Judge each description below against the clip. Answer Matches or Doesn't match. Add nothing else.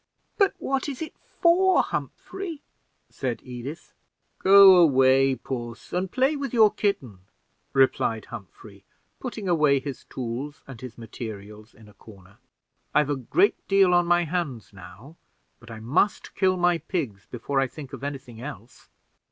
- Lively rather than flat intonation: Matches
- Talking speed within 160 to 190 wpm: Doesn't match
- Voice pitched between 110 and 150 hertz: Matches